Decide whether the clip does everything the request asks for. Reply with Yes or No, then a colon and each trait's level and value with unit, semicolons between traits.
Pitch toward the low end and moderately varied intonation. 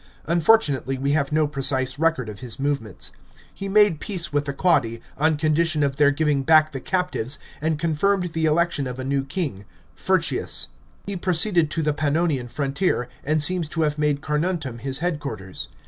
No: medium, 150 Hz; average, 3.4 semitones